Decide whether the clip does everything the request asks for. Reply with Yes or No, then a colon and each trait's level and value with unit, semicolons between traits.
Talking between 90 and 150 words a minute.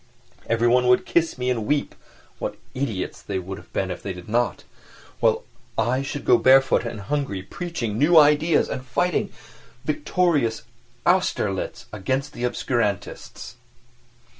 Yes: average, 140 wpm